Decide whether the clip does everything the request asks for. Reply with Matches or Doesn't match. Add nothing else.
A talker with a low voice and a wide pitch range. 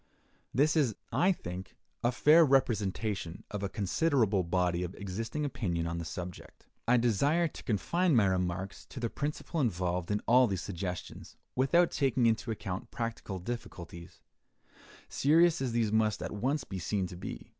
Matches